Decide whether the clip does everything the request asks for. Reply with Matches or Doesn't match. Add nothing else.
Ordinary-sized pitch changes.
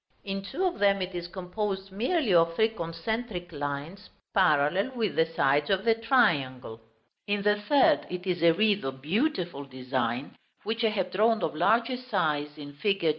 Doesn't match